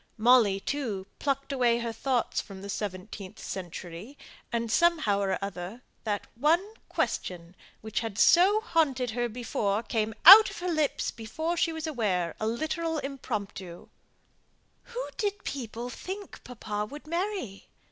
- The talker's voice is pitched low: No, high, 235 Hz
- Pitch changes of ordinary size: No, wide, 7.4 semitones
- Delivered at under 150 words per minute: Yes, average, 140 wpm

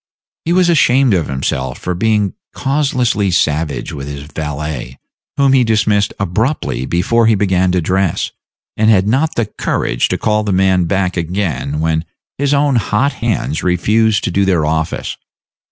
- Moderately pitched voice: No, very low, 95 Hz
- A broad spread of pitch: Yes, wide, 5.7 semitones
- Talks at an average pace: Yes, average, 160 wpm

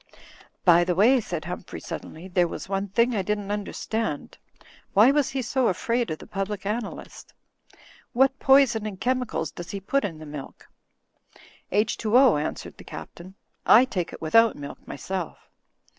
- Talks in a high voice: Yes, high, 205 Hz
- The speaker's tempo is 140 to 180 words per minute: Yes, average, 160 wpm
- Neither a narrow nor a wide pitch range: Yes, average, 5.0 semitones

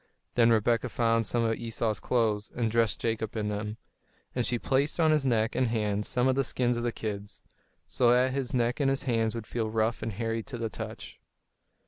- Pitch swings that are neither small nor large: No, narrow, 1.9 semitones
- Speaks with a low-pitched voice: Yes, low, 115 Hz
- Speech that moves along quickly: Yes, fast, 210 wpm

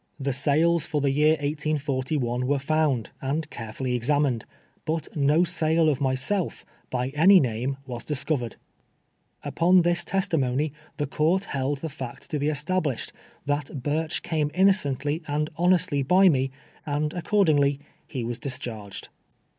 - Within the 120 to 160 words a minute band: Yes, average, 140 wpm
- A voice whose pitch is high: No, medium, 145 Hz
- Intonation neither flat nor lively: Yes, average, 3.2 semitones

